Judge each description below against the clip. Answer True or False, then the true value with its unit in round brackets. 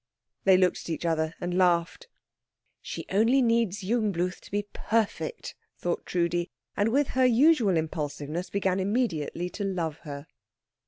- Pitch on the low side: False (185 Hz)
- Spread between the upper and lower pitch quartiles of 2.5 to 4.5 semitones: False (4.9 semitones)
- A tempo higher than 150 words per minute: False (145 wpm)